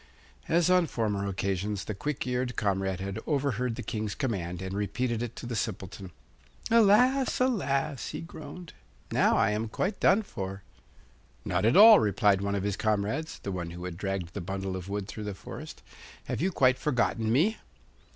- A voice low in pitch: Yes, low, 110 Hz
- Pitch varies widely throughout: Yes, wide, 6.0 semitones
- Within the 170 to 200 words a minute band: Yes, average, 180 wpm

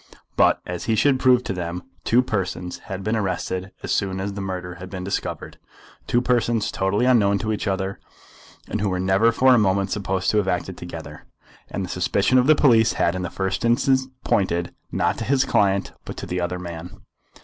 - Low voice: Yes, very low, 95 Hz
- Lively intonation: No, average, 3.8 semitones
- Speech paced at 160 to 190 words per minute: No, fast, 205 wpm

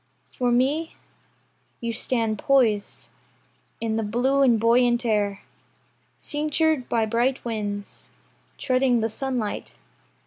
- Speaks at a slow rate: Yes, slow, 105 wpm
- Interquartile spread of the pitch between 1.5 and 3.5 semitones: Yes, average, 3.1 semitones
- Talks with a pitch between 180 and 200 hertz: No, high, 240 Hz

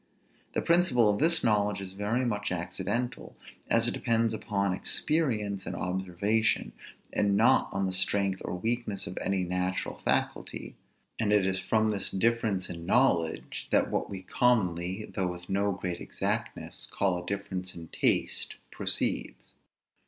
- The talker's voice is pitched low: Yes, low, 100 Hz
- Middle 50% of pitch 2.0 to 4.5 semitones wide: Yes, average, 3.3 semitones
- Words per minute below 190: Yes, average, 150 wpm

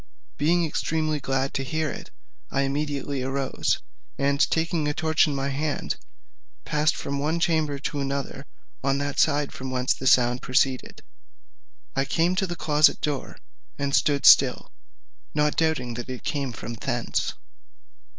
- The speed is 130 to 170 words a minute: Yes, average, 150 wpm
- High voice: No, medium, 140 Hz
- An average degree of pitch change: No, narrow, 2.3 semitones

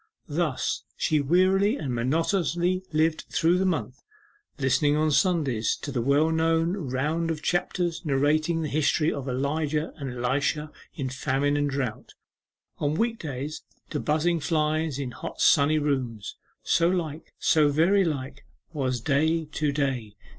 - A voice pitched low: No, medium, 150 Hz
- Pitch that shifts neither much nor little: Yes, average, 3.0 semitones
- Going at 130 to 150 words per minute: Yes, average, 145 wpm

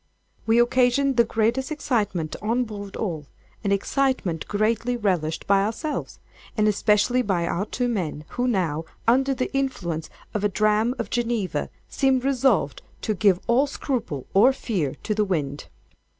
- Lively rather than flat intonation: No, average, 4.5 semitones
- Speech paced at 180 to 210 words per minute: No, average, 150 wpm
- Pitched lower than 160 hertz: No, high, 215 Hz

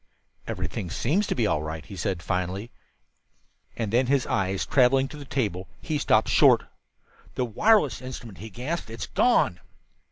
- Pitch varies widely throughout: Yes, wide, 5.7 semitones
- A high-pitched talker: No, low, 115 Hz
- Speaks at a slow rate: No, average, 160 wpm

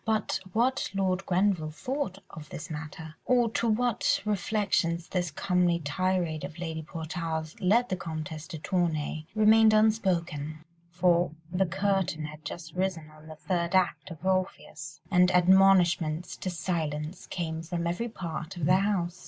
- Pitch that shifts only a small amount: No, average, 3.3 semitones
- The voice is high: No, medium, 175 Hz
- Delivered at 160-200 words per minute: No, average, 150 wpm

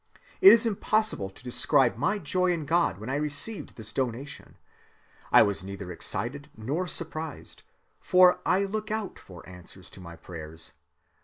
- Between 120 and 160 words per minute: Yes, average, 155 wpm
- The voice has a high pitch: No, medium, 145 Hz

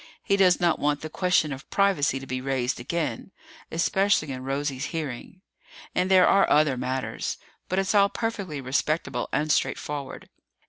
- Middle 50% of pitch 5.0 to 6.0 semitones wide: Yes, wide, 5.4 semitones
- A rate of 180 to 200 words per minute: No, average, 155 wpm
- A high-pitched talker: No, medium, 150 Hz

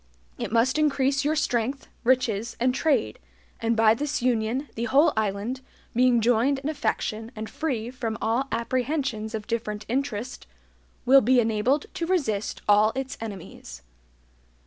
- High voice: Yes, high, 240 Hz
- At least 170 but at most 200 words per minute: No, average, 145 wpm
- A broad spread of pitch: No, average, 3.6 semitones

